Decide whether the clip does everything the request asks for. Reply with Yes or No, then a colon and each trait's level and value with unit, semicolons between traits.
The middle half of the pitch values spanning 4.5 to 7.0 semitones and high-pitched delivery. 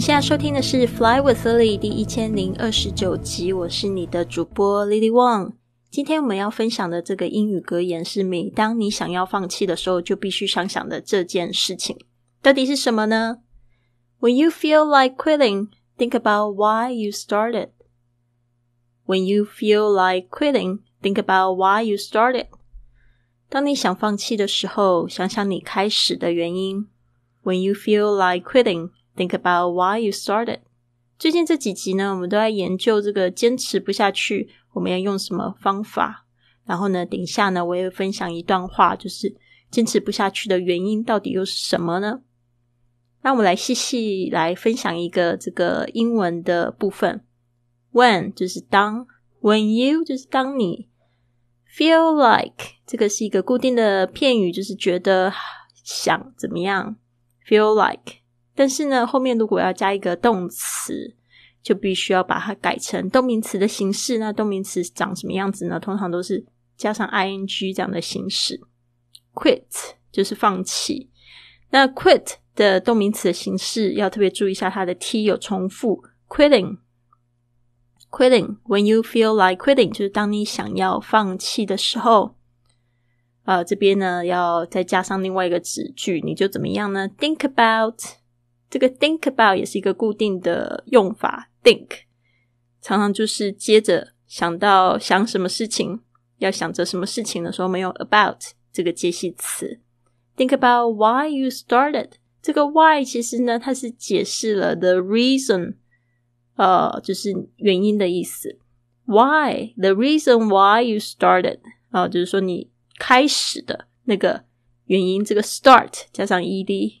No: average, 4.0 semitones; high, 195 Hz